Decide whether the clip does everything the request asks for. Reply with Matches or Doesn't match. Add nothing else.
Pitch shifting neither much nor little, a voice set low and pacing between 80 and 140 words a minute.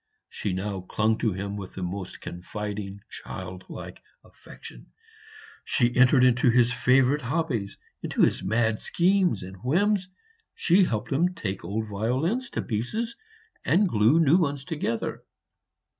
Doesn't match